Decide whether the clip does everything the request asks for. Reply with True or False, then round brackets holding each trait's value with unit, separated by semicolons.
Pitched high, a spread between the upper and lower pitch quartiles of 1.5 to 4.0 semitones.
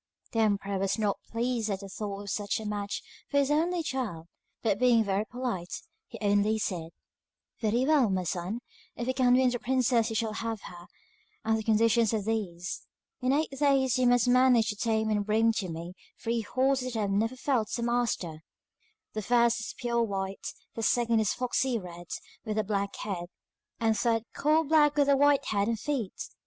True (225 Hz; 3.7 semitones)